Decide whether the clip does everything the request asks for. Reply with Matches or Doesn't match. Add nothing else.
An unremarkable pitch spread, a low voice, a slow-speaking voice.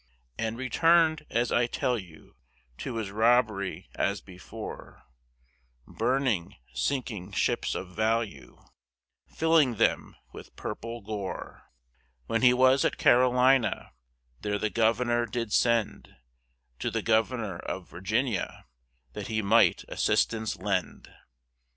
Matches